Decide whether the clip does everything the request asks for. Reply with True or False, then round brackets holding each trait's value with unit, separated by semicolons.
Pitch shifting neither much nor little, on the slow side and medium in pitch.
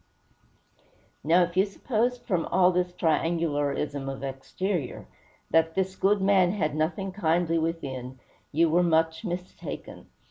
True (3.1 semitones; 130 wpm; 170 Hz)